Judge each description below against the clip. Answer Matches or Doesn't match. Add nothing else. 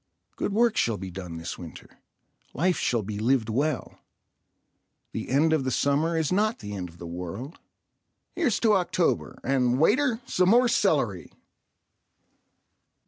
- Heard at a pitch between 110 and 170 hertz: Matches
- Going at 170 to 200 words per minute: Doesn't match